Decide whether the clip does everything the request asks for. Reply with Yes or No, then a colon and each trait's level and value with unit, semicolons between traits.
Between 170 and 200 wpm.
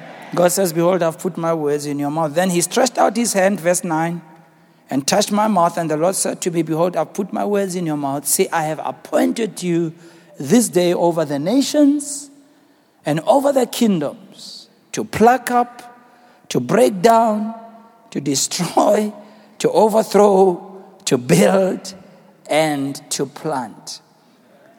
No: average, 155 wpm